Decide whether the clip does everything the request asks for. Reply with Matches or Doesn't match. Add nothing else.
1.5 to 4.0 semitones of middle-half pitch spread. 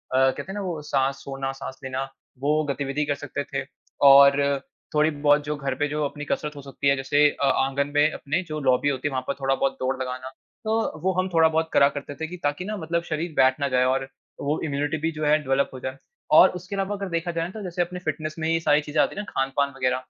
Matches